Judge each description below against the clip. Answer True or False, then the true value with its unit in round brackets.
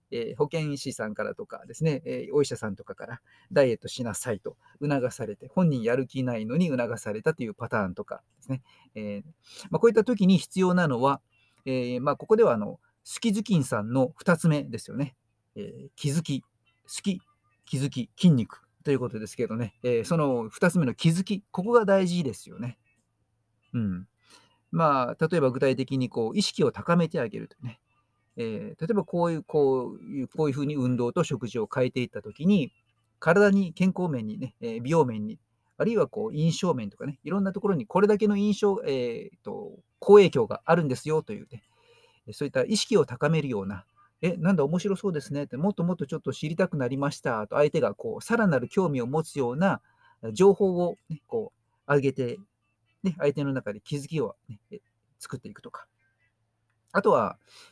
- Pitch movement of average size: False (7.0 semitones)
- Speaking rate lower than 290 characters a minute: False (365 characters per minute)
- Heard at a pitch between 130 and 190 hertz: True (140 Hz)